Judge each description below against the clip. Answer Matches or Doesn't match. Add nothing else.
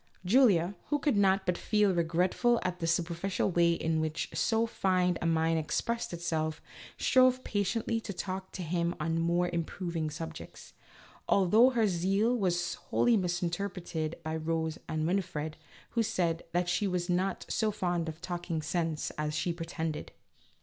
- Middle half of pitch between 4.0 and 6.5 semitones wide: Doesn't match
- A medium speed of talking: Matches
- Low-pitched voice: Doesn't match